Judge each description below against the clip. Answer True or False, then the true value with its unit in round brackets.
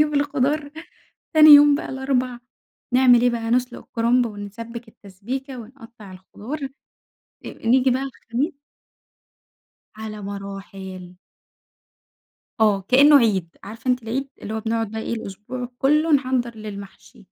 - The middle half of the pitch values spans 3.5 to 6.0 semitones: True (3.8 semitones)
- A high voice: True (235 Hz)